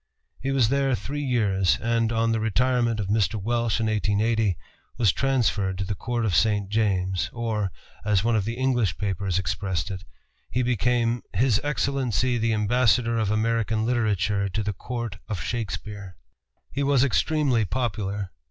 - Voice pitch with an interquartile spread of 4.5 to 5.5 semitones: No, average, 3.2 semitones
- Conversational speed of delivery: Yes, average, 160 wpm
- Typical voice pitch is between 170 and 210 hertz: No, low, 110 Hz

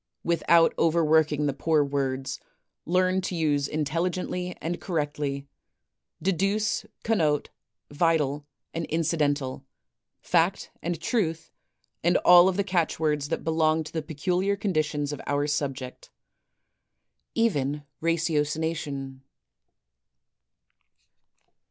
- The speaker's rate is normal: No, slow, 110 wpm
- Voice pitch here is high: No, medium, 160 Hz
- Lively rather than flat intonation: No, average, 3.2 semitones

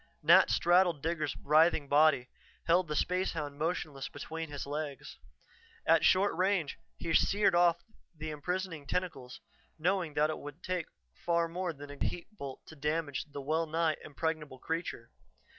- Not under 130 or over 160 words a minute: Yes, average, 150 wpm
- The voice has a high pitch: No, medium, 160 Hz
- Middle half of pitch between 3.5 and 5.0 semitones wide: No, average, 3.1 semitones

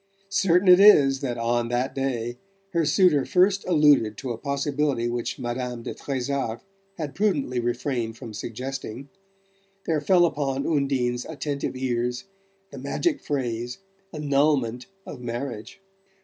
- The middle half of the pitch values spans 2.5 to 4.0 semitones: Yes, average, 3.7 semitones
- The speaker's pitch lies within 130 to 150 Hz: Yes, low, 135 Hz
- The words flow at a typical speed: No, slow, 130 wpm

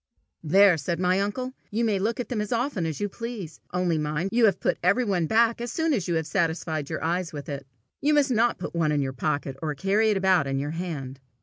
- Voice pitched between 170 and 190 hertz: Yes, medium, 185 Hz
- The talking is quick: Yes, fast, 240 wpm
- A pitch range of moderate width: No, wide, 6.1 semitones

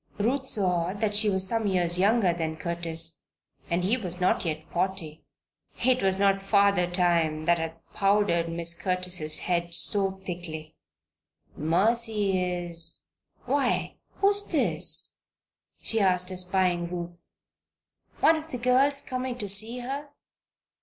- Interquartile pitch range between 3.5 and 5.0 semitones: Yes, average, 4.0 semitones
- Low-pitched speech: No, medium, 185 Hz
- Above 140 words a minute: No, slow, 135 wpm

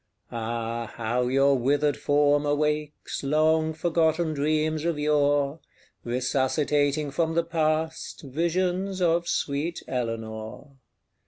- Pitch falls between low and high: Yes, medium, 150 Hz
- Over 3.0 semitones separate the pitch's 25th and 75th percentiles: No, average, 2.7 semitones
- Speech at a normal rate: No, slow, 100 wpm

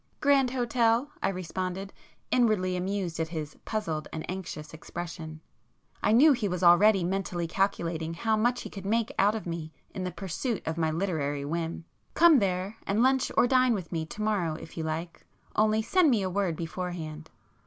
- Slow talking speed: No, average, 170 wpm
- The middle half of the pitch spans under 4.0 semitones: No, average, 4.8 semitones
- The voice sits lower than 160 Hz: No, medium, 185 Hz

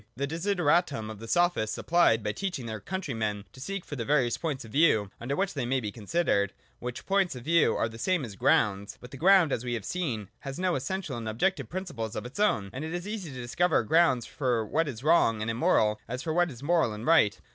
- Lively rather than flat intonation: Yes, wide, 7.3 semitones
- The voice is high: No, low, 135 Hz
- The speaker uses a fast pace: Yes, fast, 235 wpm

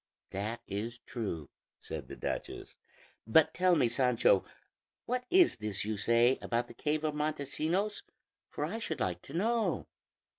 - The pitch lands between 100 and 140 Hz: Yes, low, 135 Hz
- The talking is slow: No, average, 150 wpm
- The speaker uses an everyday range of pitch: No, wide, 7.3 semitones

